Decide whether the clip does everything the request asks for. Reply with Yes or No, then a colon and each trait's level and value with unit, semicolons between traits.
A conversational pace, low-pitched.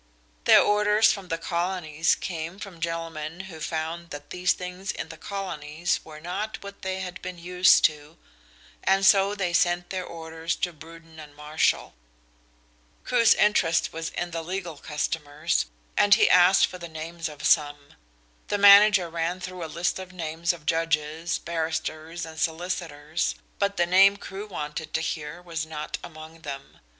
No: average, 160 wpm; medium, 170 Hz